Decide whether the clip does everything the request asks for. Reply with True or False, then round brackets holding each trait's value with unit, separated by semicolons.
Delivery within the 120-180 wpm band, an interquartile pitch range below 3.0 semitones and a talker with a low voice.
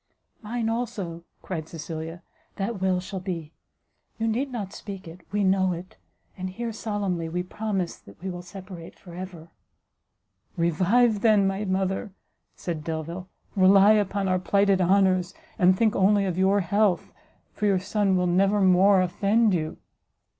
False (155 wpm; 2.4 semitones; 190 Hz)